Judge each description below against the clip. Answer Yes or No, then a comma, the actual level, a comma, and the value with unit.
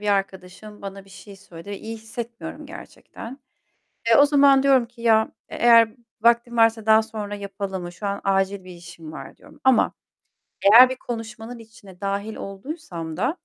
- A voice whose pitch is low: No, high, 220 Hz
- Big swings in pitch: No, average, 3.2 semitones